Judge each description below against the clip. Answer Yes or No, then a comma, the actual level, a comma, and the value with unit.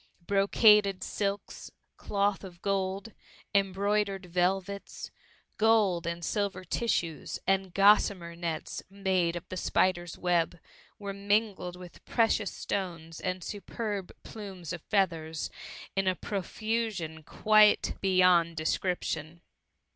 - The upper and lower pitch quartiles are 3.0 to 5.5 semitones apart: No, narrow, 2.6 semitones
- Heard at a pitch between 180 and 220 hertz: Yes, high, 190 Hz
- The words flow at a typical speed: No, slow, 115 wpm